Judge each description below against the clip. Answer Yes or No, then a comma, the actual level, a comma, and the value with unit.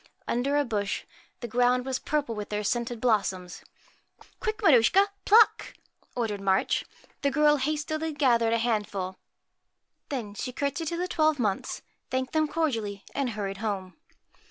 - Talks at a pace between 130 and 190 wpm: Yes, average, 155 wpm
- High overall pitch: Yes, high, 245 Hz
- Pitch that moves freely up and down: Yes, wide, 6.0 semitones